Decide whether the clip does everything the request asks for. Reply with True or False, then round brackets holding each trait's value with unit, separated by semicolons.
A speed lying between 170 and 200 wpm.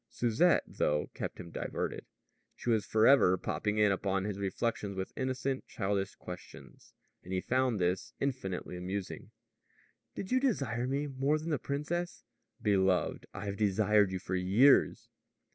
False (145 wpm)